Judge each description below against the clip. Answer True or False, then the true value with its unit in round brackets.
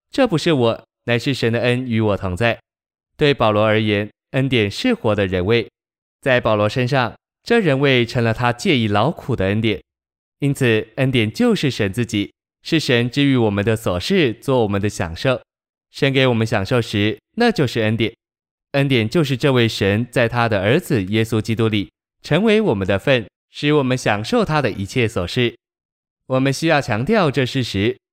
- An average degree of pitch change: True (4.3 semitones)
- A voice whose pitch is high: False (120 Hz)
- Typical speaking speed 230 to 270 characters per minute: True (260 characters per minute)